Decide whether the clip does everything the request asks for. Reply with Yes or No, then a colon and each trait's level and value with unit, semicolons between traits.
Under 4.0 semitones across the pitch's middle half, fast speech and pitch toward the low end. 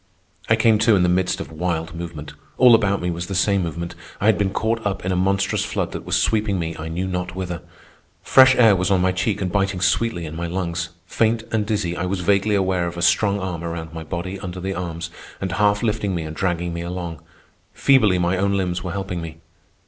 Yes: average, 2.7 semitones; fast, 230 wpm; very low, 90 Hz